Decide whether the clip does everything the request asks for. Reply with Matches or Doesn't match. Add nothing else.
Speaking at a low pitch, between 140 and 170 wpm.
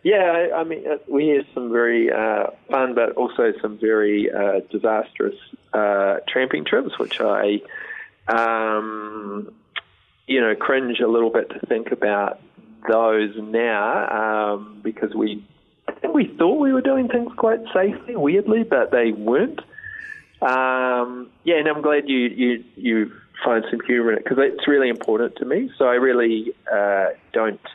Matches